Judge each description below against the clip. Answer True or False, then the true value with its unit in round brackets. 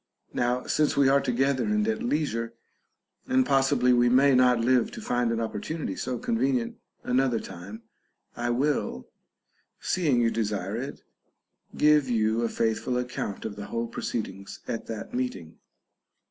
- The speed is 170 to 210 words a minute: False (150 wpm)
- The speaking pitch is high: False (125 Hz)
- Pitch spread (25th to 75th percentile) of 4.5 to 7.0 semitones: False (3.1 semitones)